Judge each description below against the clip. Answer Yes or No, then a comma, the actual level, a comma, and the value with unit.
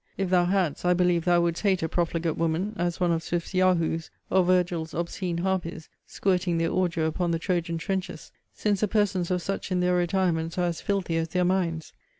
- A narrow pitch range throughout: Yes, narrow, 1.8 semitones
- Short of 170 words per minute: No, average, 200 wpm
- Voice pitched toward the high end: No, medium, 175 Hz